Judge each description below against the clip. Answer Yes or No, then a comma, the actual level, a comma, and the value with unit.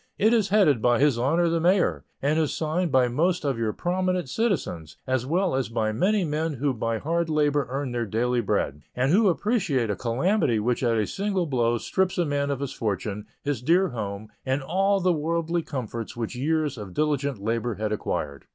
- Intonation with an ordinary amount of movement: No, wide, 6.6 semitones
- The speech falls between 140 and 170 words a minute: No, average, 200 wpm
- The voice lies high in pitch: No, medium, 140 Hz